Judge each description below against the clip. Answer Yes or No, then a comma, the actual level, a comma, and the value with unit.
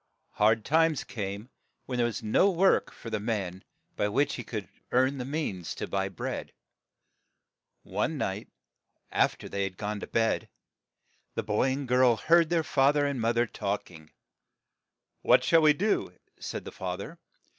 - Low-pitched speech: Yes, low, 120 Hz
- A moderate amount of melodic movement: No, wide, 5.8 semitones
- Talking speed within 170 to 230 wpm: Yes, average, 175 wpm